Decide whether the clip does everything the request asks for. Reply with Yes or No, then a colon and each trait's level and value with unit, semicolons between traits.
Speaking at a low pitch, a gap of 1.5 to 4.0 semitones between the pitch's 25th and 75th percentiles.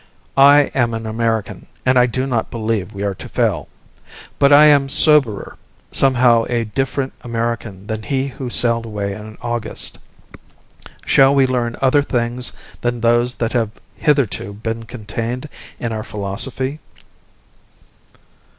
Yes: low, 120 Hz; average, 2.9 semitones